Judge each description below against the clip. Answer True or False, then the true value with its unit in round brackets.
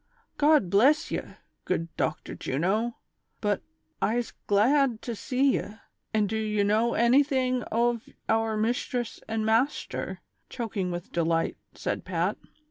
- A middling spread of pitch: True (3.4 semitones)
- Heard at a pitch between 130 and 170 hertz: False (225 Hz)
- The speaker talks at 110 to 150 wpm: True (140 wpm)